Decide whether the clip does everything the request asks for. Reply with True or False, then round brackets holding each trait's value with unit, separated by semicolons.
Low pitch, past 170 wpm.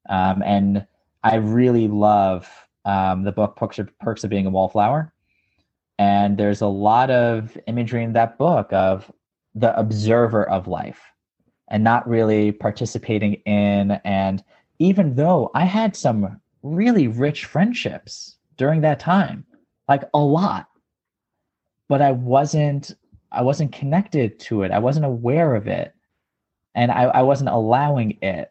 False (115 Hz; 145 wpm)